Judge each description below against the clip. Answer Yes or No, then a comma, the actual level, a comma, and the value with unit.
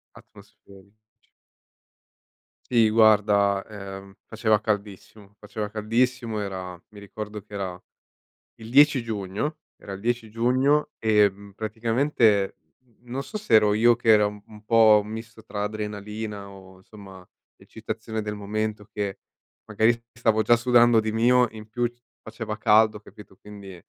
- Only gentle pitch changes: Yes, narrow, 2.0 semitones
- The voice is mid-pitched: No, low, 110 Hz